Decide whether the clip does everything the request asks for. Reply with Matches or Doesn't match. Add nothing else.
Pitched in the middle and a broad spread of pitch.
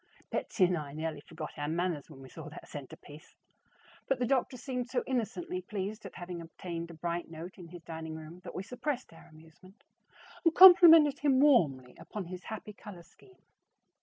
Matches